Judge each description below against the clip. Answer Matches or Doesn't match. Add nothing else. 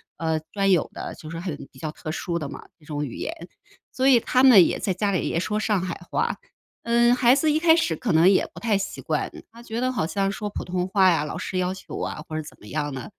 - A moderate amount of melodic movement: Doesn't match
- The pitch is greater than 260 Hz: Doesn't match